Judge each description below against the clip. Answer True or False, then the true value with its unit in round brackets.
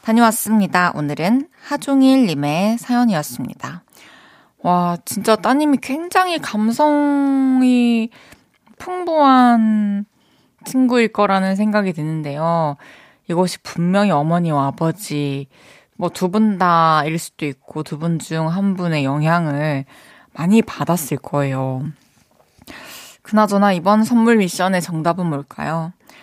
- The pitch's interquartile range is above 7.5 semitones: False (6.4 semitones)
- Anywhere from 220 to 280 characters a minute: True (240 characters per minute)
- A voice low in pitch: False (195 Hz)